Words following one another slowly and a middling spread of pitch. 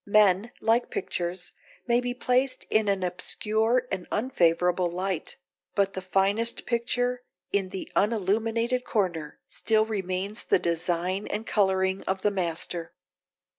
Yes: slow, 130 wpm; average, 3.8 semitones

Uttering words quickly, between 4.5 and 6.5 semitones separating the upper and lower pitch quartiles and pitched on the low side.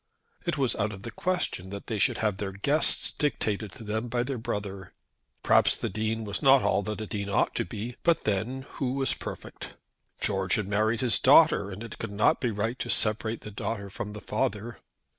No: fast, 210 wpm; average, 3.1 semitones; low, 110 Hz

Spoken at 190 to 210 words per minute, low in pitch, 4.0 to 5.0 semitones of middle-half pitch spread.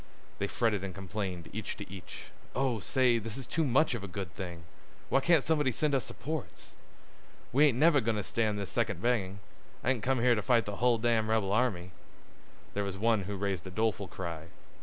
Yes: fast, 205 wpm; low, 110 Hz; average, 4.4 semitones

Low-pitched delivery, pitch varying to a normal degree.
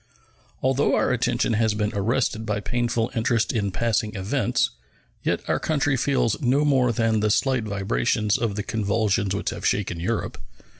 Yes: low, 115 Hz; average, 3.0 semitones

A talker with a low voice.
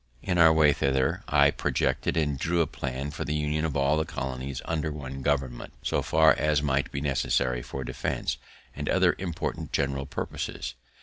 Yes: very low, 70 Hz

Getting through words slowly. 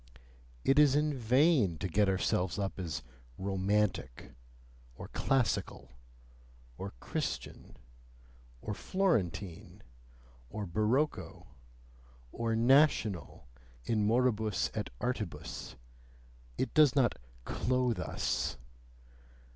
Yes: slow, 90 wpm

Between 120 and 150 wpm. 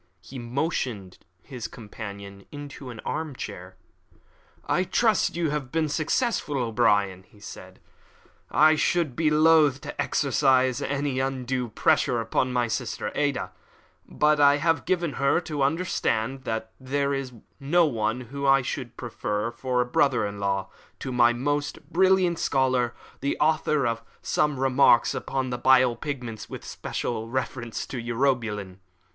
Yes: average, 145 wpm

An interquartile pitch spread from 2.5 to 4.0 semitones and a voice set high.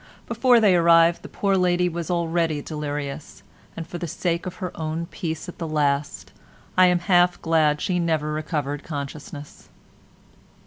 No: average, 2.8 semitones; medium, 165 Hz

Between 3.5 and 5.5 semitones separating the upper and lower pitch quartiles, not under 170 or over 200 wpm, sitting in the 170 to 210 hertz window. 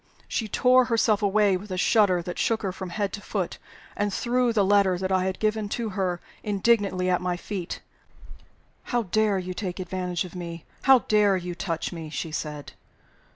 No: average, 3.0 semitones; average, 190 wpm; high, 190 Hz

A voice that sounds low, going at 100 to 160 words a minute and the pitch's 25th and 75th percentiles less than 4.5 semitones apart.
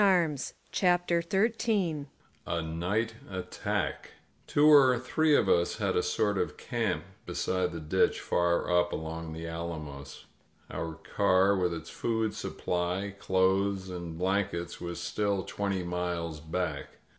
No: very low, 95 Hz; average, 140 wpm; average, 5.2 semitones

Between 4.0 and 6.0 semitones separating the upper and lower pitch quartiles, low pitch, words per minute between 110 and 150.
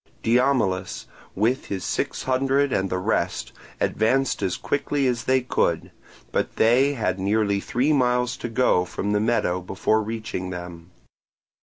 Yes: average, 5.2 semitones; low, 115 Hz; average, 145 wpm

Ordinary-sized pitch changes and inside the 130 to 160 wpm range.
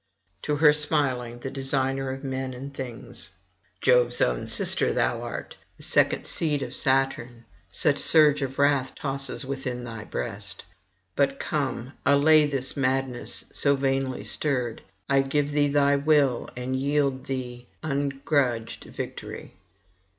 No: narrow, 1.9 semitones; slow, 135 wpm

